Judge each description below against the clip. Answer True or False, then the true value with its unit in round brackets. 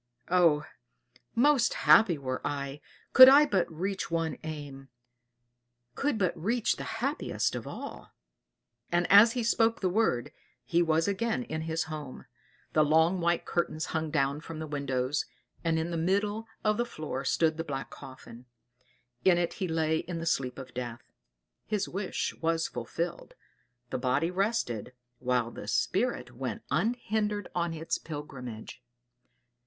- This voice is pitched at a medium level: True (165 Hz)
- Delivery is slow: False (150 wpm)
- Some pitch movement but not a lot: False (5.8 semitones)